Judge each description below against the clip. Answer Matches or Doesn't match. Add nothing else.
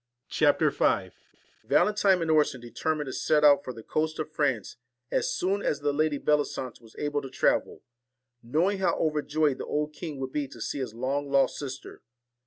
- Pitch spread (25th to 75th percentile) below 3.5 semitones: Matches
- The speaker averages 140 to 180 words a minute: Doesn't match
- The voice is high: Doesn't match